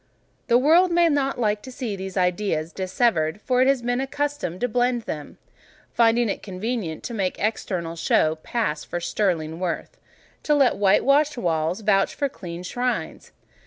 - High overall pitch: Yes, high, 215 Hz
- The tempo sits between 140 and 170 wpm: Yes, average, 160 wpm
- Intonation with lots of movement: Yes, wide, 5.9 semitones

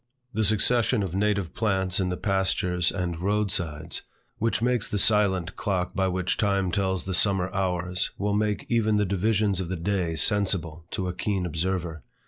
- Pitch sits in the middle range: No, very low, 95 Hz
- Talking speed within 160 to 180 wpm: Yes, average, 170 wpm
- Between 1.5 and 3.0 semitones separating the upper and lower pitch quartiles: Yes, narrow, 2.5 semitones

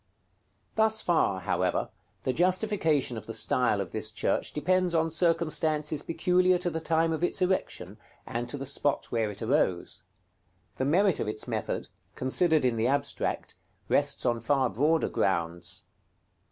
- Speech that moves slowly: No, average, 160 wpm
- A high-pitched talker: No, medium, 150 Hz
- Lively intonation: Yes, wide, 6.8 semitones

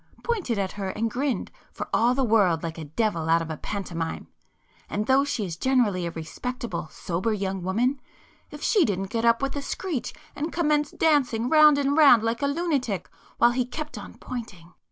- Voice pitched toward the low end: No, high, 230 Hz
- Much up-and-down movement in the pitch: Yes, wide, 6.8 semitones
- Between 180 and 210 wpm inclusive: Yes, average, 195 wpm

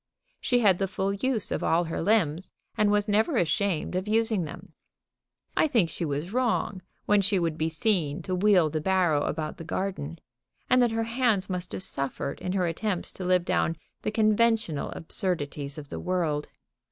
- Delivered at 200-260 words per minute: No, average, 185 wpm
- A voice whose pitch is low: No, medium, 185 Hz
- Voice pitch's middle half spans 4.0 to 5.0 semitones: Yes, average, 4.7 semitones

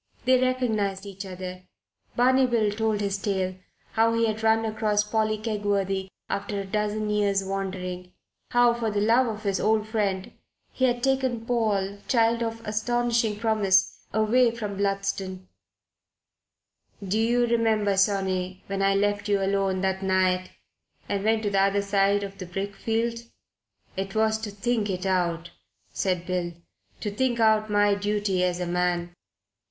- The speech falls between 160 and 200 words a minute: No, average, 150 wpm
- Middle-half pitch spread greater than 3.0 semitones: No, narrow, 2.5 semitones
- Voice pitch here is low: No, high, 205 Hz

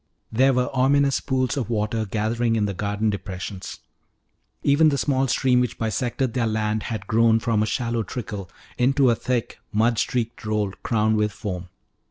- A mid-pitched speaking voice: No, low, 115 Hz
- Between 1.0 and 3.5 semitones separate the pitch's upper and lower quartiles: Yes, average, 2.9 semitones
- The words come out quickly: No, average, 170 wpm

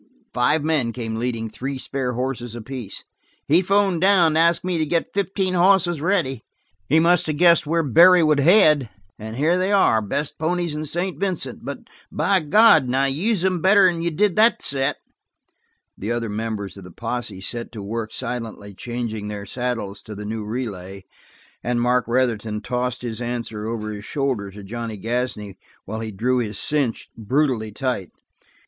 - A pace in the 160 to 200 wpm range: Yes, average, 175 wpm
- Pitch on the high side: No, low, 125 Hz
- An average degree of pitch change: No, wide, 6.9 semitones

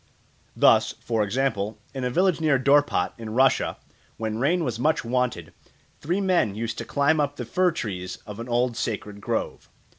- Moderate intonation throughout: Yes, average, 4.9 semitones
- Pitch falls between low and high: No, low, 125 Hz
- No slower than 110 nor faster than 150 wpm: No, average, 175 wpm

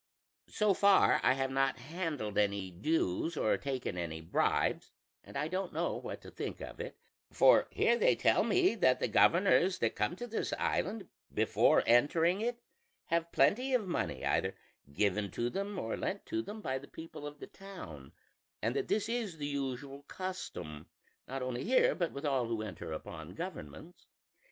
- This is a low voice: No, medium, 145 Hz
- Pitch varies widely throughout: Yes, wide, 8.7 semitones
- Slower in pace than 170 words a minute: No, average, 175 wpm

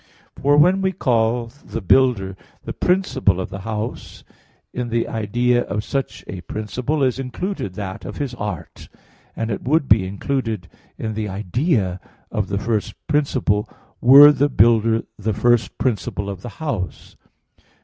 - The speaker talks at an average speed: Yes, average, 150 wpm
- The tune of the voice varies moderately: Yes, average, 4.6 semitones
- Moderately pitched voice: No, low, 115 Hz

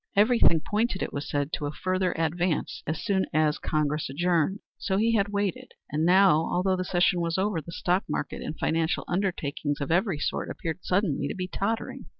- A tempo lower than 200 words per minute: Yes, average, 190 wpm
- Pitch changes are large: No, average, 3.7 semitones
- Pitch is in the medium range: Yes, medium, 175 Hz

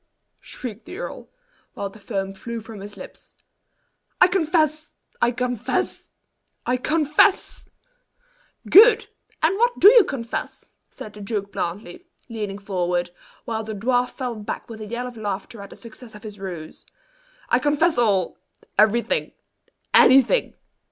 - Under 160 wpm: Yes, average, 140 wpm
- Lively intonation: Yes, wide, 5.8 semitones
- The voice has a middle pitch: No, high, 230 Hz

